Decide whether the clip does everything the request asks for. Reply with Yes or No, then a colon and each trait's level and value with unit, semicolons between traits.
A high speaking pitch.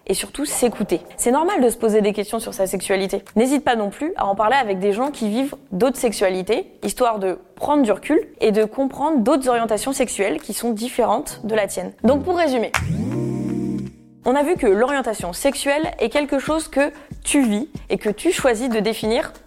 Yes: high, 235 Hz